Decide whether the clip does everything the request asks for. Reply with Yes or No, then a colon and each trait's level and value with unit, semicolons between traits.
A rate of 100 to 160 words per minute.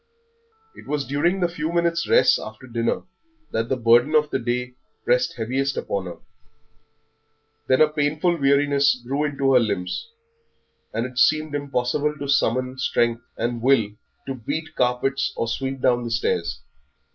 Yes: average, 155 wpm